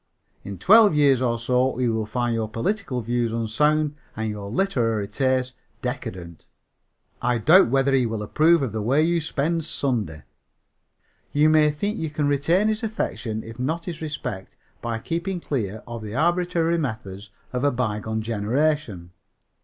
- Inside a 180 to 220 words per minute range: No, average, 160 wpm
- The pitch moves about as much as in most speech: No, wide, 5.9 semitones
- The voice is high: No, low, 125 Hz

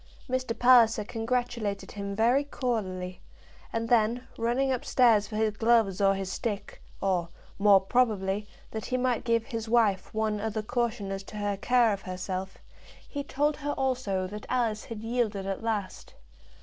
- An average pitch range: Yes, average, 3.4 semitones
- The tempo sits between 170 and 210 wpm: No, average, 160 wpm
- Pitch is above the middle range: Yes, high, 220 Hz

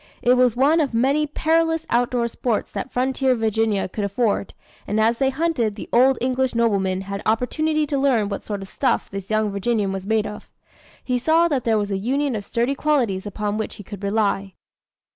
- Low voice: No, high, 230 Hz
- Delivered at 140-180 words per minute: No, average, 200 wpm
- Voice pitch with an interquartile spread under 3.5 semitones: No, average, 4.5 semitones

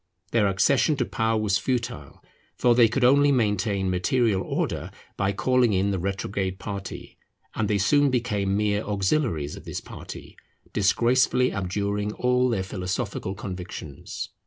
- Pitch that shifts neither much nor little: Yes, average, 4.0 semitones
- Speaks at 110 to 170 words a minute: Yes, average, 140 wpm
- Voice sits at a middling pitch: No, low, 105 Hz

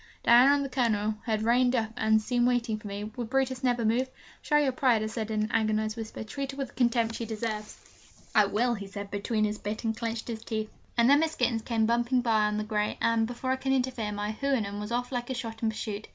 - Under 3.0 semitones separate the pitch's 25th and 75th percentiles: Yes, narrow, 2.5 semitones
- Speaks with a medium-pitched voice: No, high, 230 Hz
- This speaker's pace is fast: Yes, fast, 245 wpm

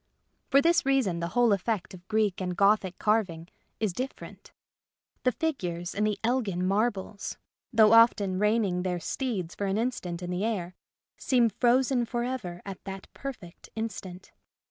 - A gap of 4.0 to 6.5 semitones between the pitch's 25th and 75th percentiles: Yes, average, 4.7 semitones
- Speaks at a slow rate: No, average, 155 wpm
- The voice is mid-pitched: No, high, 210 Hz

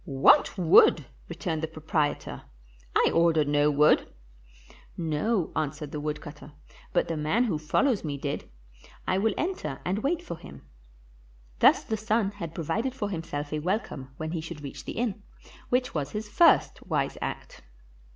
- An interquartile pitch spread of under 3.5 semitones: No, wide, 5.6 semitones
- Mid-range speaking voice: Yes, medium, 160 Hz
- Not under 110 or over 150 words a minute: No, average, 170 wpm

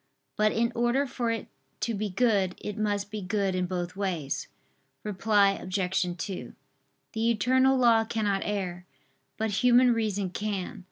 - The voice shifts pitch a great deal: No, average, 3.3 semitones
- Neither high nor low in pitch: No, high, 210 Hz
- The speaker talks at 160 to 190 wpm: No, average, 150 wpm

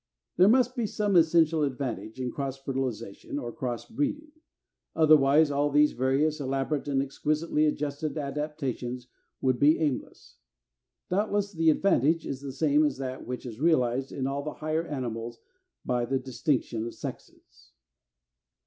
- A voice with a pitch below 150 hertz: Yes, medium, 140 Hz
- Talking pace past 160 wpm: No, average, 150 wpm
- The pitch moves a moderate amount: Yes, average, 3.4 semitones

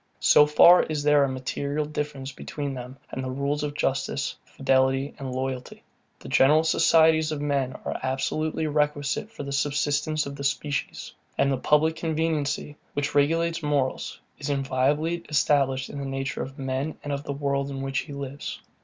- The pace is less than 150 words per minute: No, average, 170 wpm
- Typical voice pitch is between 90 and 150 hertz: Yes, medium, 140 Hz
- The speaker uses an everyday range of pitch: No, narrow, 1.8 semitones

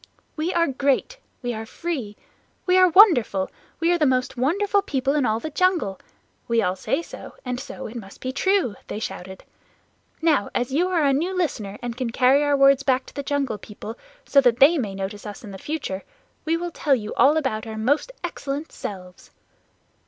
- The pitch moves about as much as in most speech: No, wide, 6.6 semitones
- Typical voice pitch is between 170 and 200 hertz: No, very high, 270 Hz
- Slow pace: No, average, 195 wpm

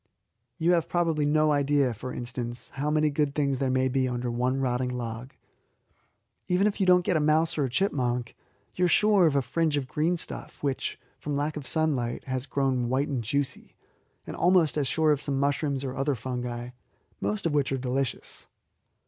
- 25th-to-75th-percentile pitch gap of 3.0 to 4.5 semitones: Yes, average, 3.4 semitones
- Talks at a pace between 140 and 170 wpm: No, average, 195 wpm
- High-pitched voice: No, medium, 140 Hz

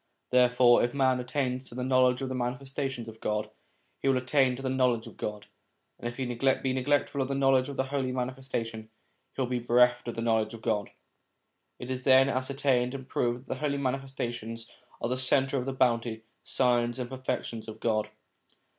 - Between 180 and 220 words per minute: Yes, average, 200 wpm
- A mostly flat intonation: Yes, narrow, 1.9 semitones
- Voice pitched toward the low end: Yes, low, 125 Hz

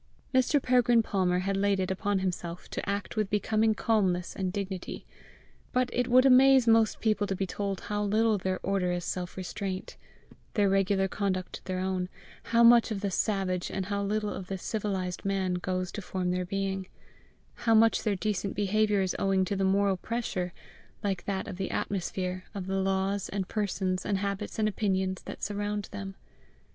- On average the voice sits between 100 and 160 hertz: No, high, 195 Hz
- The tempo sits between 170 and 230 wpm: Yes, average, 180 wpm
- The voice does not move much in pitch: Yes, narrow, 2.0 semitones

